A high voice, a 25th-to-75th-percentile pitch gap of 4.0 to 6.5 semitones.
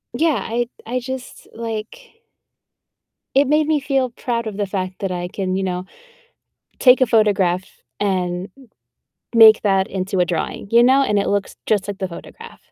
Yes: high, 215 Hz; average, 5.0 semitones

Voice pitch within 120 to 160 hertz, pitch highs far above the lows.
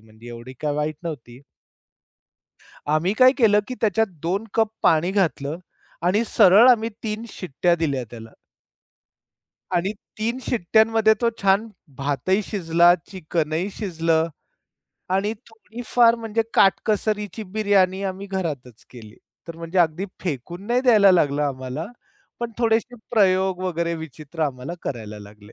No: medium, 180 Hz; wide, 6.0 semitones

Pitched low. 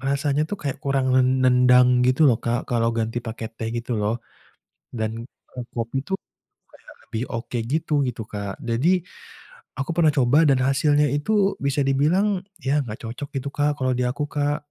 Yes: low, 130 Hz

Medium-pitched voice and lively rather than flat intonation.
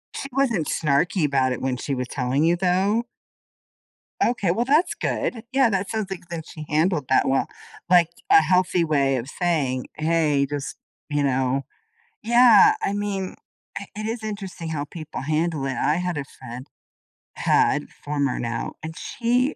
Yes: medium, 165 Hz; wide, 6.3 semitones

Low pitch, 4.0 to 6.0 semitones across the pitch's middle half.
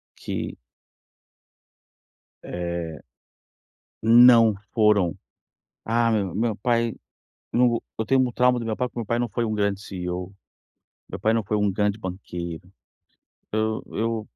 No: low, 110 Hz; average, 3.4 semitones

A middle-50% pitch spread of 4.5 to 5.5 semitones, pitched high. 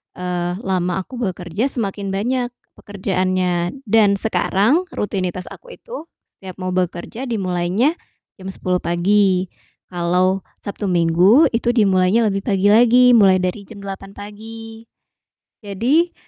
No: average, 3.6 semitones; high, 195 Hz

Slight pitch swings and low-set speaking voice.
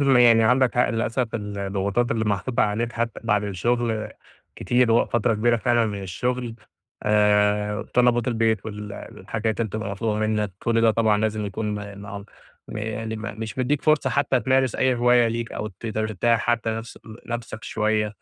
Yes: narrow, 2.2 semitones; low, 110 Hz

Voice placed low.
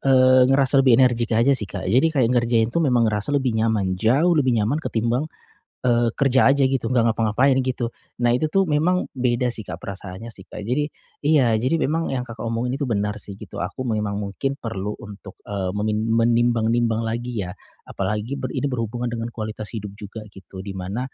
Yes: low, 115 Hz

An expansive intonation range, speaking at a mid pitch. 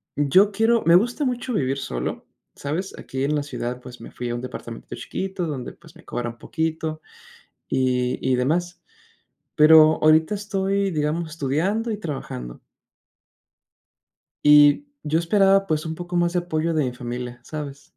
Yes: wide, 5.7 semitones; medium, 155 Hz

